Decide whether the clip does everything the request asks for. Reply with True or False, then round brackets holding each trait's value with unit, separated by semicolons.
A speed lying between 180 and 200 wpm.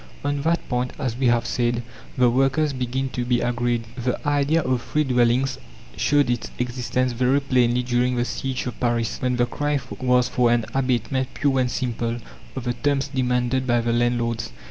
True (185 wpm)